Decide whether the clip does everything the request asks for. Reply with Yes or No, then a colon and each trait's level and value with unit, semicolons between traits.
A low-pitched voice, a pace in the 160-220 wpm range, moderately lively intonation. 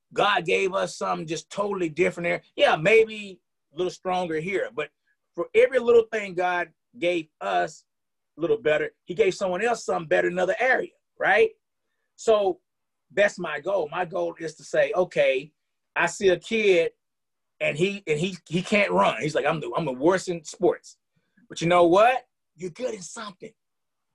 No: medium, 185 Hz; average, 180 wpm; average, 4.5 semitones